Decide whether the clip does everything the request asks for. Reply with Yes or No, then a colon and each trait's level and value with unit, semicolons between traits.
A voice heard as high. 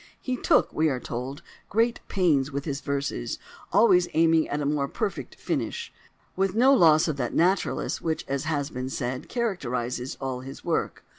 No: medium, 150 Hz